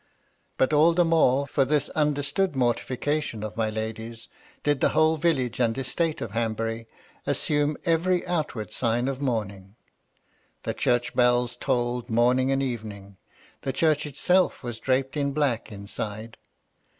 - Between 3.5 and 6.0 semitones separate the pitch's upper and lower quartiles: Yes, average, 4.6 semitones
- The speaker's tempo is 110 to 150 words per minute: Yes, average, 140 wpm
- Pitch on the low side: Yes, low, 130 Hz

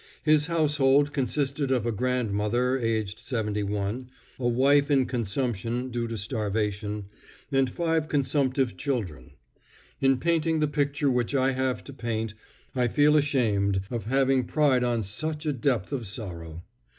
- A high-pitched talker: No, low, 125 Hz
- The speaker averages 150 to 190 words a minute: No, average, 140 wpm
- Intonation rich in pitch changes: No, average, 4.3 semitones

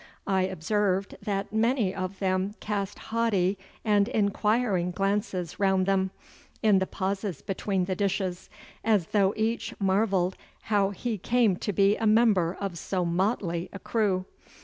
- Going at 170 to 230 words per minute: No, average, 145 wpm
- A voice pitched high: Yes, high, 195 Hz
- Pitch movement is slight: Yes, narrow, 2.1 semitones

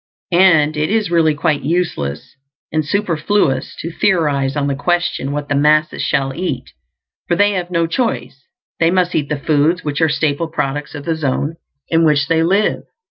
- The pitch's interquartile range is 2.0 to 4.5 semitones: Yes, average, 3.4 semitones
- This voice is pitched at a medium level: Yes, medium, 155 Hz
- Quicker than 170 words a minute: Yes, average, 180 wpm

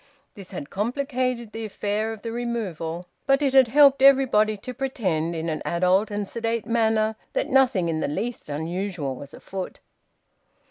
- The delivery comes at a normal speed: Yes, average, 165 wpm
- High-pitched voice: Yes, high, 215 Hz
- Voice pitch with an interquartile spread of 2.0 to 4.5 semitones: No, average, 5.2 semitones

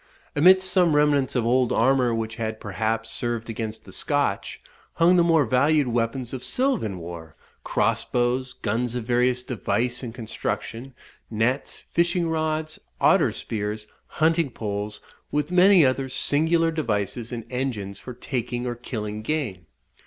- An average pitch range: Yes, average, 4.9 semitones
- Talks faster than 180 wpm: No, average, 145 wpm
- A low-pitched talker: Yes, low, 125 Hz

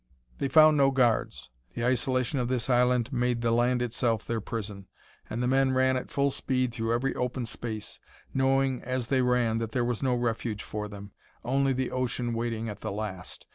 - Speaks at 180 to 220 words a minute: Yes, average, 195 wpm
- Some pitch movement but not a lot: No, narrow, 2.2 semitones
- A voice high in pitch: No, low, 125 Hz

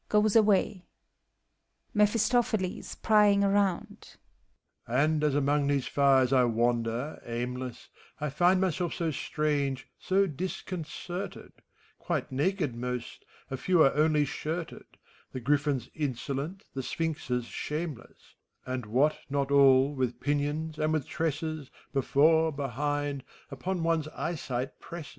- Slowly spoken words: Yes, slow, 115 wpm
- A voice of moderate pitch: Yes, medium, 150 Hz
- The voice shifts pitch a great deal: No, average, 4.3 semitones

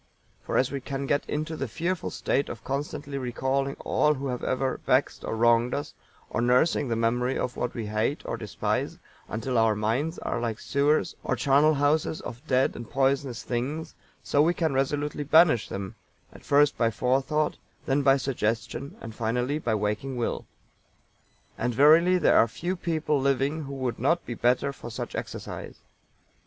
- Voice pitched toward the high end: No, low, 135 Hz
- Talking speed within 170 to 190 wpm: Yes, average, 175 wpm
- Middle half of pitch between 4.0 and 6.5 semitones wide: No, average, 3.5 semitones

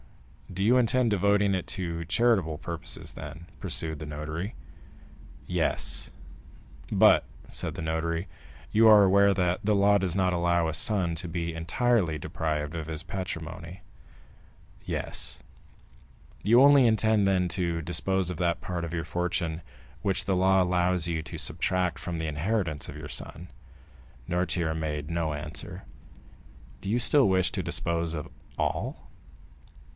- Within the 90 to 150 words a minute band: Yes, average, 145 wpm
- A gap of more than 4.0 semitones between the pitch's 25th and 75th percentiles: No, average, 3.2 semitones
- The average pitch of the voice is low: Yes, very low, 90 Hz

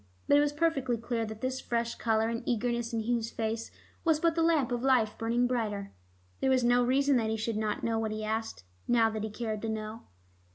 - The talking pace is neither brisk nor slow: No, fast, 230 wpm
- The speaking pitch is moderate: No, high, 230 Hz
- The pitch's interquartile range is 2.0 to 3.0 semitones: Yes, narrow, 2.4 semitones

